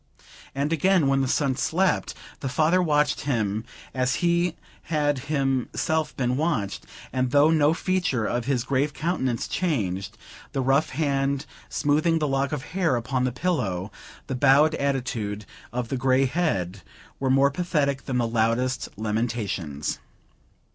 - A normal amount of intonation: Yes, average, 3.8 semitones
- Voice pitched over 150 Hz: No, low, 135 Hz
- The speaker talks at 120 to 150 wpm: Yes, average, 145 wpm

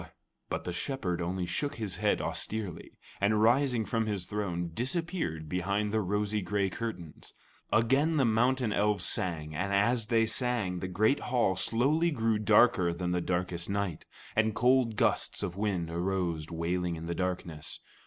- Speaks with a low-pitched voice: Yes, low, 100 Hz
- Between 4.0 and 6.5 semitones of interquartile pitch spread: Yes, average, 4.4 semitones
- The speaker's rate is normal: Yes, average, 160 wpm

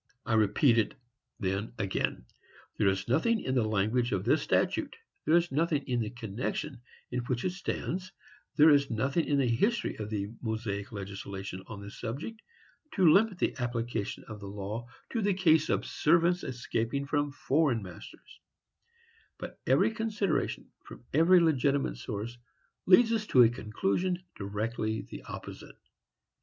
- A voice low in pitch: Yes, low, 125 Hz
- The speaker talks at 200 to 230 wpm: No, average, 155 wpm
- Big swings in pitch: Yes, wide, 7.0 semitones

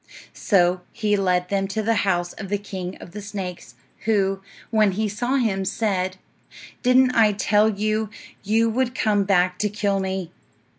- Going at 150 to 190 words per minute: Yes, average, 165 wpm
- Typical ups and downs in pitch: No, narrow, 2.3 semitones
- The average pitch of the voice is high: Yes, high, 200 Hz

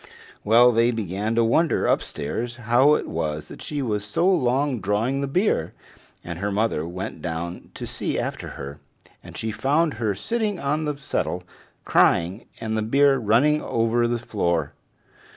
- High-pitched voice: No, low, 115 Hz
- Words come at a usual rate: Yes, average, 165 wpm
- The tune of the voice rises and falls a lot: Yes, wide, 5.9 semitones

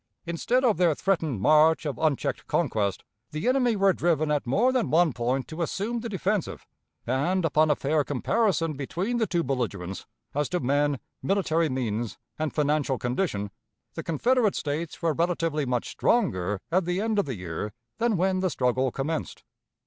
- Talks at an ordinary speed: Yes, average, 170 wpm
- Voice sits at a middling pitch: Yes, medium, 155 Hz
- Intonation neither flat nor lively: No, wide, 6.0 semitones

